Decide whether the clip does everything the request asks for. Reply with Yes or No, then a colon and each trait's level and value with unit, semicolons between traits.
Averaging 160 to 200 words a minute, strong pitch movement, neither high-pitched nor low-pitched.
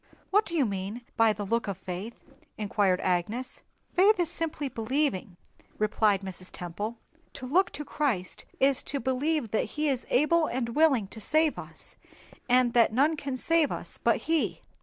No: average, 170 wpm; wide, 6.3 semitones; very high, 250 Hz